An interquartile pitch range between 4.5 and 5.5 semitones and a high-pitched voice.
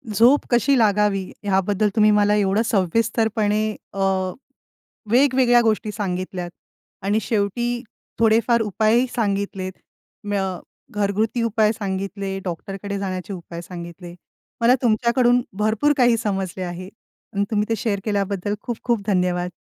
No: average, 2.9 semitones; high, 210 Hz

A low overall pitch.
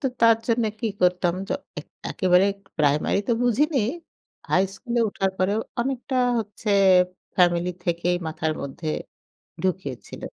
No: high, 190 Hz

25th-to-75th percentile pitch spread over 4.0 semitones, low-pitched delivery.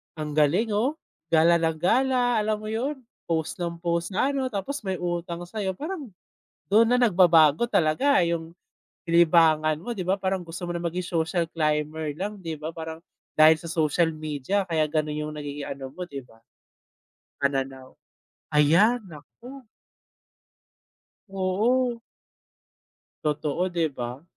No: average, 5.0 semitones; medium, 170 Hz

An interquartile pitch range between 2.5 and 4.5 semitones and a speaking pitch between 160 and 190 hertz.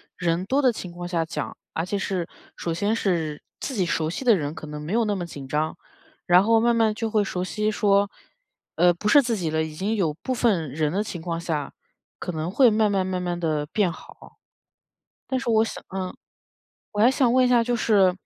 No: average, 4.9 semitones; medium, 185 Hz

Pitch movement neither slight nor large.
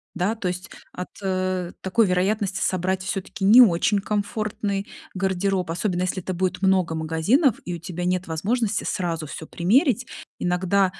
No: narrow, 2.3 semitones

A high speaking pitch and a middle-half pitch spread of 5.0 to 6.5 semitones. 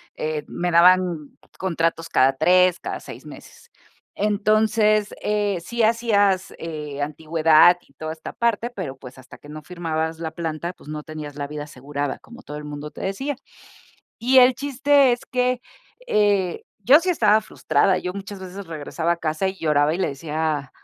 No: medium, 175 Hz; wide, 5.4 semitones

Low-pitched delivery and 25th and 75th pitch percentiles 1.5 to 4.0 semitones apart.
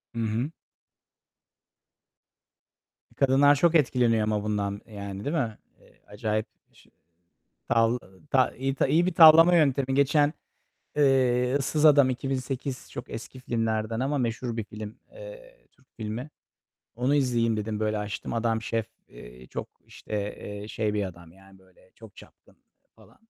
No: low, 120 Hz; average, 4.4 semitones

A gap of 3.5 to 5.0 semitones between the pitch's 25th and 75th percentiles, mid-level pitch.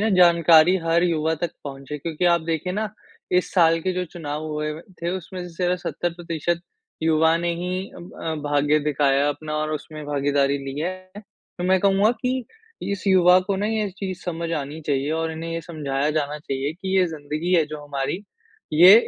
No: average, 3.1 semitones; medium, 165 Hz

